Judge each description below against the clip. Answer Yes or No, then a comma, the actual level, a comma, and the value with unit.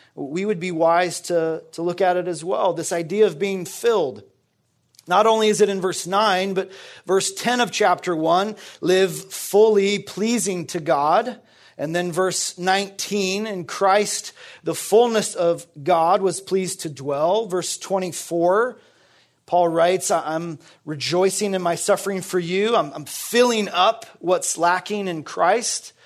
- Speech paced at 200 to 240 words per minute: No, average, 155 wpm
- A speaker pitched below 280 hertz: Yes, medium, 185 Hz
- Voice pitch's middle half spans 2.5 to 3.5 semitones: Yes, average, 2.9 semitones